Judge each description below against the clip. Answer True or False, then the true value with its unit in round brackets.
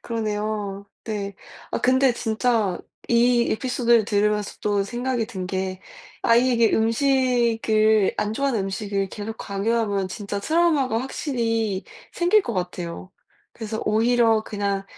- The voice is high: True (220 Hz)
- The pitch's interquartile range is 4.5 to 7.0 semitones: False (3.0 semitones)